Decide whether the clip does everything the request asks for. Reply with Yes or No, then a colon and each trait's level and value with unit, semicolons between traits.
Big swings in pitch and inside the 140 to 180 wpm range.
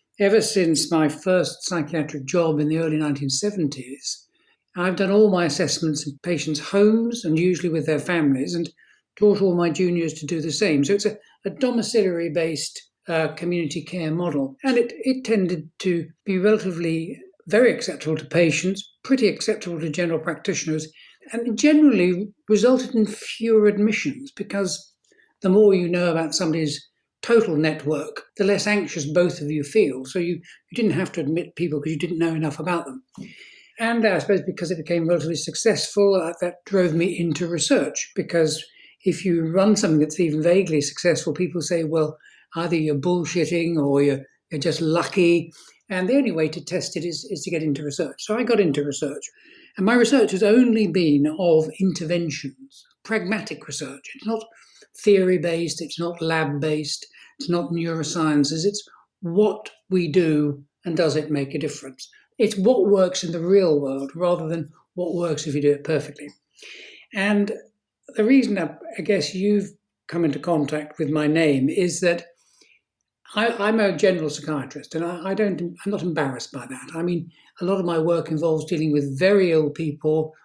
No: average, 4.2 semitones; average, 175 wpm